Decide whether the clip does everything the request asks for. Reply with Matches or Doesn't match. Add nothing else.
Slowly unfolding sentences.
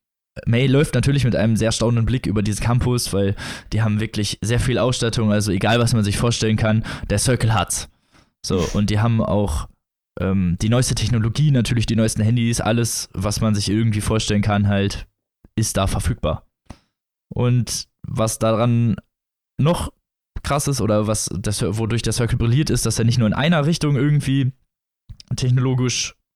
Doesn't match